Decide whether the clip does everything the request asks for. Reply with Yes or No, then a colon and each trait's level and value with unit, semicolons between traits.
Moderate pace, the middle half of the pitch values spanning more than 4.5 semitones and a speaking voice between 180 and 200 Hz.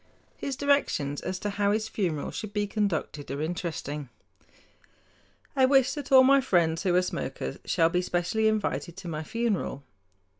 Yes: average, 160 wpm; average, 5.3 semitones; high, 190 Hz